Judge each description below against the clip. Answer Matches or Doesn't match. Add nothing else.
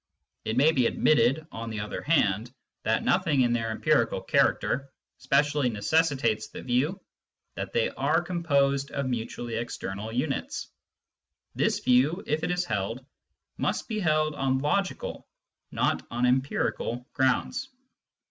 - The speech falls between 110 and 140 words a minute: Matches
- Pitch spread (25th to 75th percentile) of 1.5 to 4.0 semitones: Doesn't match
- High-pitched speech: Doesn't match